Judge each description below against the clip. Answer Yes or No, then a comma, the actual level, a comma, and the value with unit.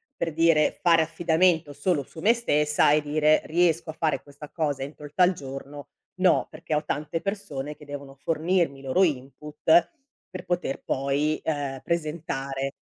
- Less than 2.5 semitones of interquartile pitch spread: No, average, 2.8 semitones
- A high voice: No, medium, 150 Hz